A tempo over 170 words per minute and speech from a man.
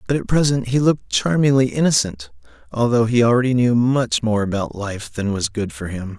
Yes: average, 195 wpm; male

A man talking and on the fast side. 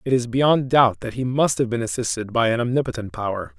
Yes: male; fast, 235 wpm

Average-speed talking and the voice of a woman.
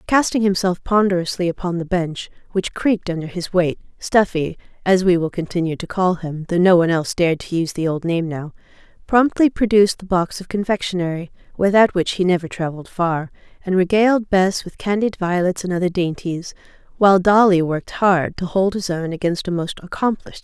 Yes: average, 180 wpm; female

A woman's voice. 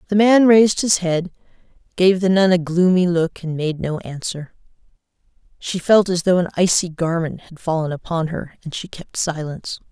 Yes: female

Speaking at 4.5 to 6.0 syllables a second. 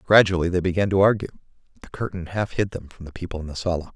No: 7.3 syllables/s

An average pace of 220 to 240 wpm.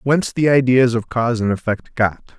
No: average, 200 wpm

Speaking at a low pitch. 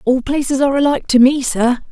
No: very high, 265 Hz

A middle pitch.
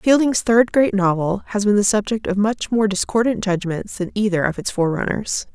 No: high, 205 Hz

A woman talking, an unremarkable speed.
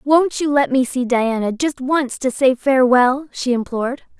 Yes: female; average, 185 wpm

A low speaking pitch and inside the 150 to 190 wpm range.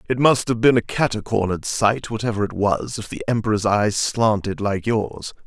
Yes: low, 110 Hz; average, 185 wpm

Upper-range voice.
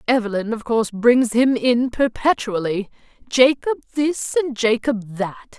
Yes: high, 235 Hz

